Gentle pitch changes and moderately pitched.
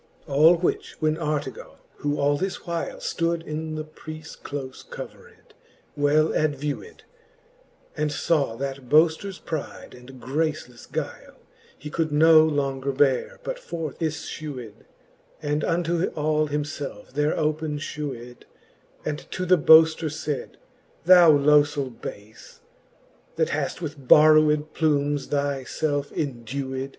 Yes: narrow, 2.1 semitones; medium, 150 Hz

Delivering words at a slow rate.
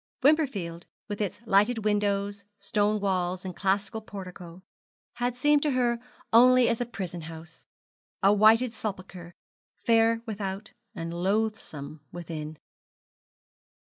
Yes: slow, 115 wpm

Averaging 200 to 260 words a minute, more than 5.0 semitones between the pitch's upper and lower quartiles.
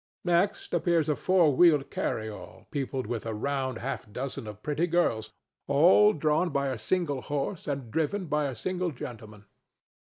No: average, 160 wpm; wide, 5.6 semitones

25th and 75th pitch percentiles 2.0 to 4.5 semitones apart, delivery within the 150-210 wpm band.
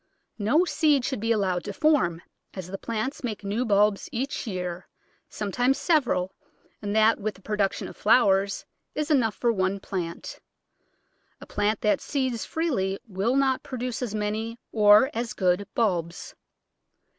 Yes: average, 4.2 semitones; average, 155 wpm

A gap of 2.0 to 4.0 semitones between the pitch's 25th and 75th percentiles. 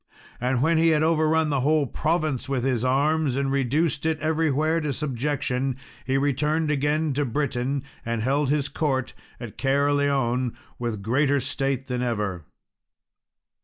Yes: average, 3.0 semitones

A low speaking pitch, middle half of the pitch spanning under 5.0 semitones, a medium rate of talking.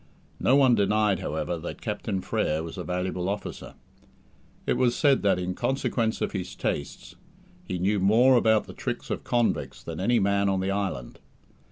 Yes: low, 100 Hz; average, 3.7 semitones; average, 175 wpm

